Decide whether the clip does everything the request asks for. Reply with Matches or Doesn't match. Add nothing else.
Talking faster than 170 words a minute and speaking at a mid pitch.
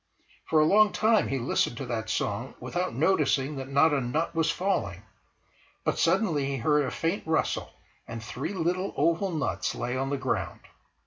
Matches